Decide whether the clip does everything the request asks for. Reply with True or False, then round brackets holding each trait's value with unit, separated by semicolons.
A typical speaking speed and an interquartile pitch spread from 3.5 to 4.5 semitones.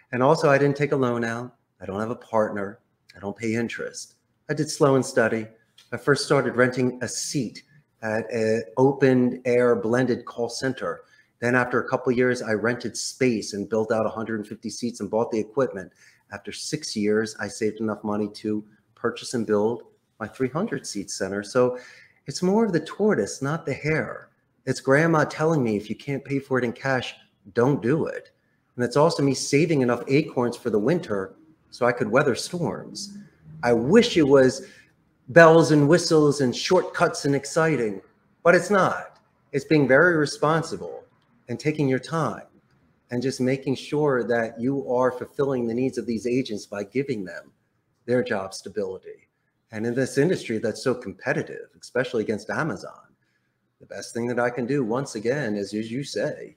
True (180 wpm; 4.0 semitones)